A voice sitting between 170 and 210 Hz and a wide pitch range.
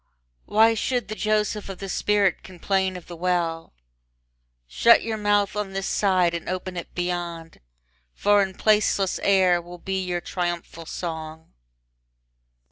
No: medium, 185 Hz; average, 2.8 semitones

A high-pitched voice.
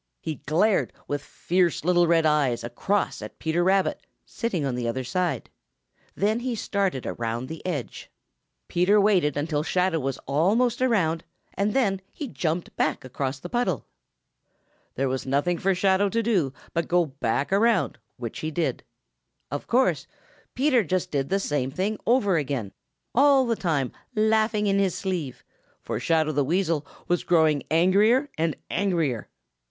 No: medium, 175 Hz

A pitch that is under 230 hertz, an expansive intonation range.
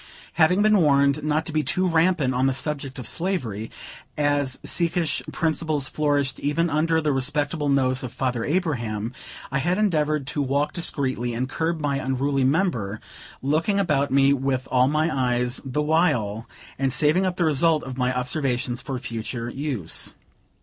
No: medium, 140 Hz; average, 3.6 semitones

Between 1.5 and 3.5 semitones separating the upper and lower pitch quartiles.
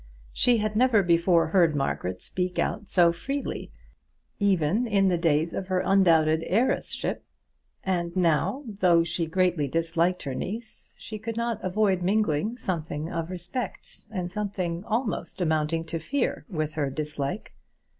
No: average, 4.3 semitones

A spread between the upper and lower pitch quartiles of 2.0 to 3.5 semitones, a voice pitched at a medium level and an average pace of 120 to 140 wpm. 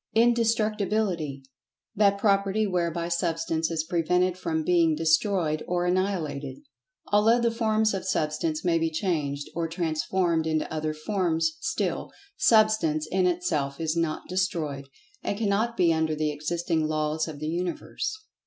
No: average, 4.0 semitones; medium, 170 Hz; slow, 135 wpm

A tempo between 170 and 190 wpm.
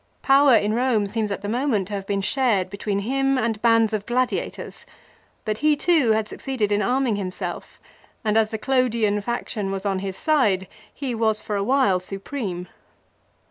Yes: average, 180 wpm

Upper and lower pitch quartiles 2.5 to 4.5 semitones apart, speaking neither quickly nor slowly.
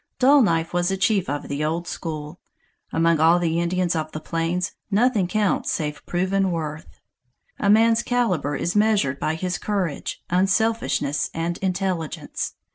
Yes: average, 3.6 semitones; average, 150 wpm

